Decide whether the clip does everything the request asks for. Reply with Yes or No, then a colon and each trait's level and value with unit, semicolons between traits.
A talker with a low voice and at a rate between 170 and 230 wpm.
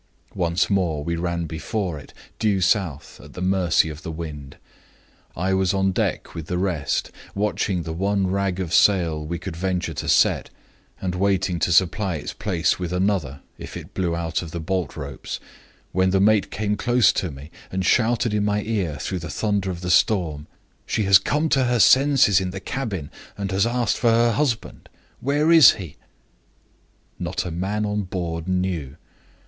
Yes: very low, 95 Hz; average, 185 wpm